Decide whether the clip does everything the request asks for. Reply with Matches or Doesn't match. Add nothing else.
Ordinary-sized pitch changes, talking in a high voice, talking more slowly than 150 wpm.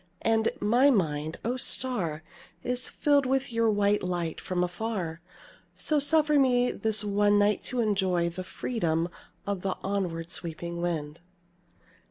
Doesn't match